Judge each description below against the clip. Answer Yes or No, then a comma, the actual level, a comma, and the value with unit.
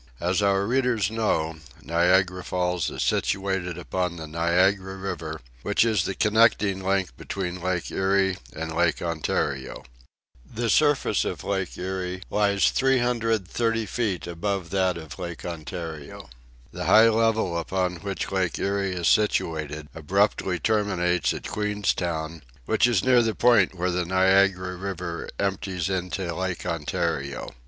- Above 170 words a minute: No, slow, 135 wpm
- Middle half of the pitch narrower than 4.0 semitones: Yes, average, 2.7 semitones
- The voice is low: Yes, very low, 95 Hz